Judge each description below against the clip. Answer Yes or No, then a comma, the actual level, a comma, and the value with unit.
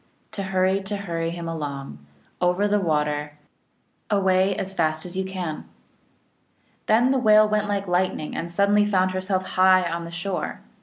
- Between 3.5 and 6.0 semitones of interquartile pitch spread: No, average, 3.0 semitones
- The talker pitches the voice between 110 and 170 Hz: No, medium, 185 Hz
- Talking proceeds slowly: No, average, 165 wpm